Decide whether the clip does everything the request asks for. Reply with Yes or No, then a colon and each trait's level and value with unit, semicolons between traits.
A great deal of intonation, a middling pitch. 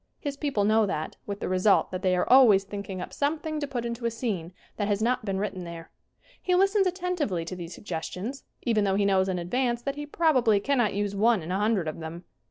No: wide, 5.8 semitones; high, 210 Hz